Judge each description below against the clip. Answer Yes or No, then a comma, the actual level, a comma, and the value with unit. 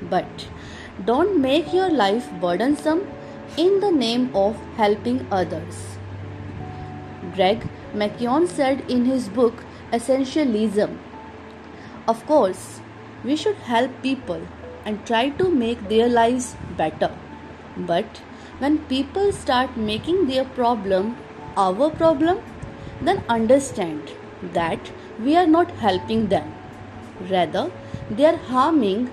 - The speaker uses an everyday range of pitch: No, wide, 6.1 semitones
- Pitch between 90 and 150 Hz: No, very high, 250 Hz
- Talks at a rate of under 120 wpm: Yes, slow, 110 wpm